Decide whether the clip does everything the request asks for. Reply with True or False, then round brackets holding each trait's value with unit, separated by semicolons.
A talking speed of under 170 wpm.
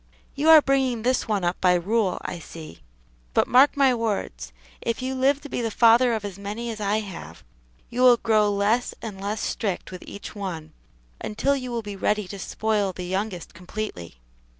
False (195 wpm)